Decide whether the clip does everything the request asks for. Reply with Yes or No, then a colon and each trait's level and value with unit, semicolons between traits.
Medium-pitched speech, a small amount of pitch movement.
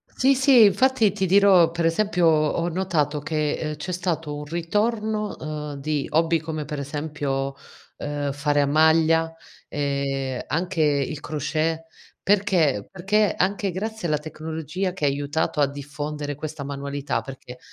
No: medium, 155 Hz; average, 3.8 semitones